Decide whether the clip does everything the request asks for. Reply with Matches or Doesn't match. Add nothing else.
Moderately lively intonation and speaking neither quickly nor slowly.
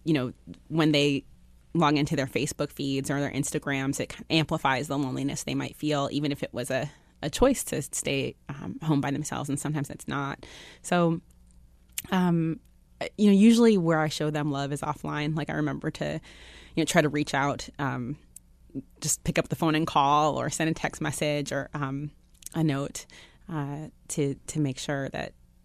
Doesn't match